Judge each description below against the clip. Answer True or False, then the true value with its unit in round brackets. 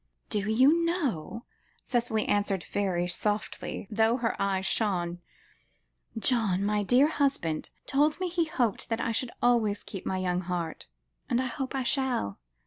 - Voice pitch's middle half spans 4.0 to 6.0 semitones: True (5.3 semitones)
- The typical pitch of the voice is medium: False (220 Hz)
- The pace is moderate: True (145 wpm)